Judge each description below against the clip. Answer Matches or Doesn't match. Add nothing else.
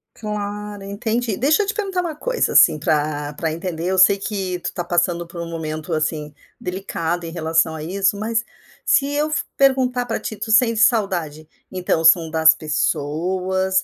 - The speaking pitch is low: Doesn't match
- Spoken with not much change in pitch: Doesn't match